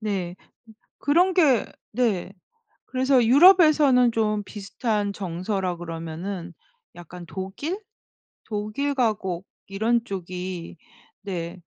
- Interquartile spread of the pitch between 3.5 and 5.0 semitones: No, wide, 5.6 semitones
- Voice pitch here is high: Yes, high, 205 Hz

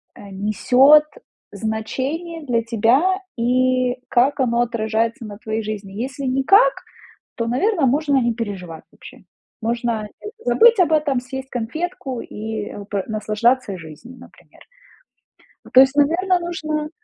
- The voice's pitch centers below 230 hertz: No, very high, 250 Hz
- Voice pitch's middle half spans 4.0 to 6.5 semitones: Yes, average, 4.8 semitones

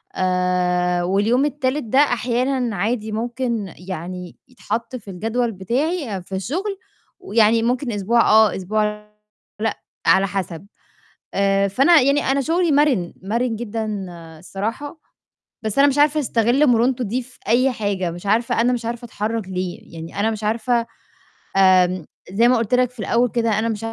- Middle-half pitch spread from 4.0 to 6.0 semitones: Yes, average, 4.4 semitones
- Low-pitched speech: No, high, 225 Hz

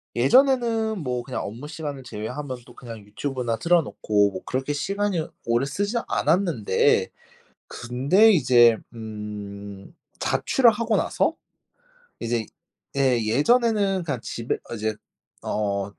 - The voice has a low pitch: Yes, low, 130 Hz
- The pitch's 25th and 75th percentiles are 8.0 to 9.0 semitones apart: Yes, wide, 8.6 semitones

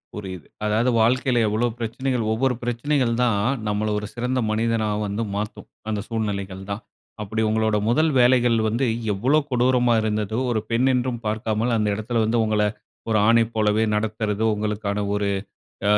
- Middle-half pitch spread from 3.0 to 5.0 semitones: No, narrow, 2.4 semitones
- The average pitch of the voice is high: No, low, 110 Hz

